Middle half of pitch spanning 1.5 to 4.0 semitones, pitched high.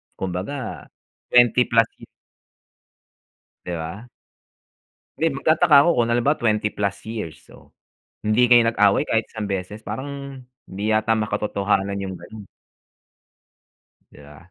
No: average, 3.5 semitones; low, 110 Hz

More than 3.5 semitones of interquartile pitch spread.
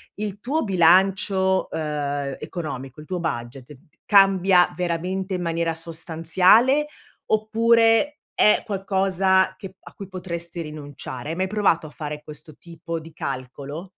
Yes: average, 3.9 semitones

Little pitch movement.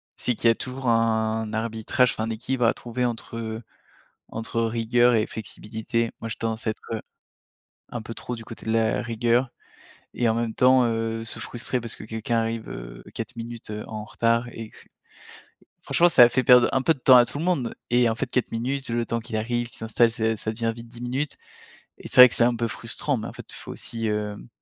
Yes: narrow, 1.5 semitones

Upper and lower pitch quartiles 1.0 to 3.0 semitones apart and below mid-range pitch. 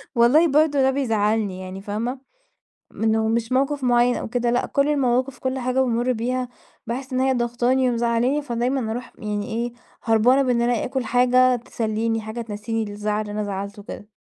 No: narrow, 2.6 semitones; high, 240 Hz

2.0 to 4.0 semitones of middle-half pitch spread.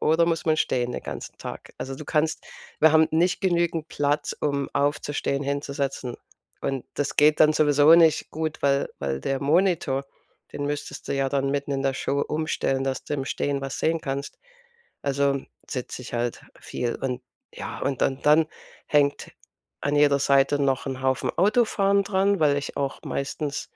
Yes: narrow, 2.4 semitones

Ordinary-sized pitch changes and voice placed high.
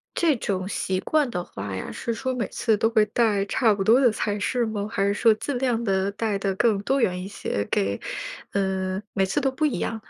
Yes: average, 3.6 semitones; high, 210 Hz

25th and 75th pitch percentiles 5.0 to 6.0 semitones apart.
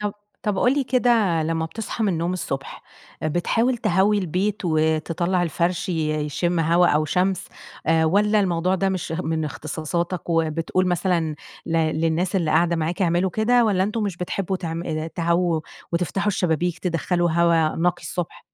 No: average, 2.7 semitones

